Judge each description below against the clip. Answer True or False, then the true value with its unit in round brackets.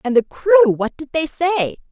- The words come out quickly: True (220 wpm)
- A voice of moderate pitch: False (270 Hz)